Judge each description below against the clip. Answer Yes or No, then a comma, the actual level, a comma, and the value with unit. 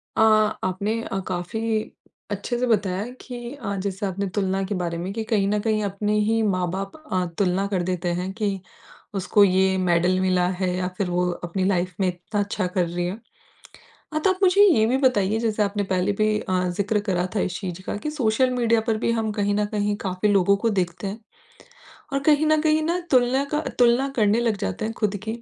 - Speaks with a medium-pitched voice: No, high, 205 Hz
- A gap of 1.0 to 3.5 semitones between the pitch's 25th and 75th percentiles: Yes, average, 3.2 semitones